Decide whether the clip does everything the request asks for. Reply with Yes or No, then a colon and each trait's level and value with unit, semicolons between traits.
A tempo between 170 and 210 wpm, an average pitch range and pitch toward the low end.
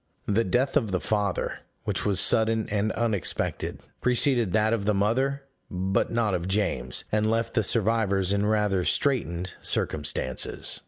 No: average, 150 wpm; average, 3.0 semitones; low, 105 Hz